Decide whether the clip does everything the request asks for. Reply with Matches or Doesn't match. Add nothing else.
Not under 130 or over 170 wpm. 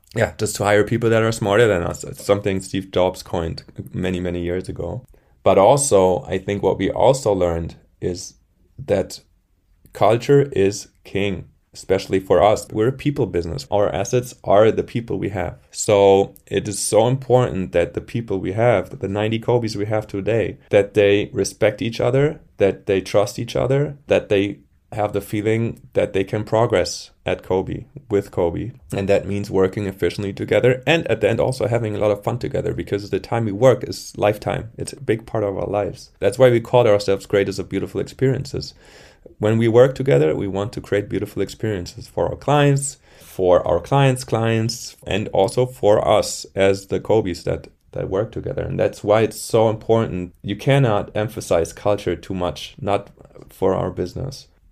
Doesn't match